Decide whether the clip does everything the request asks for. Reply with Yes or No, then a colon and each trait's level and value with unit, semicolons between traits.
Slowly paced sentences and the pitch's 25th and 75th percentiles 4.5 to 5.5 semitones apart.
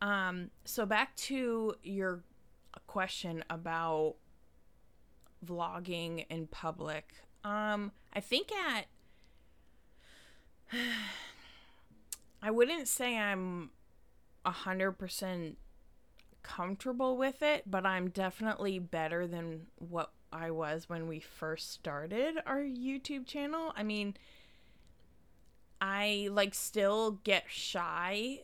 Yes: slow, 95 wpm; average, 5.2 semitones